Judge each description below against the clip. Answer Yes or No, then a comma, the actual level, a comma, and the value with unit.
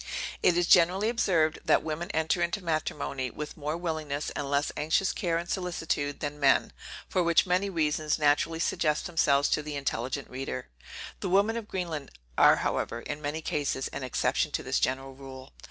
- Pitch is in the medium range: Yes, medium, 155 Hz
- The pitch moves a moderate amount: Yes, average, 3.4 semitones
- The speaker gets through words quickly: No, average, 175 wpm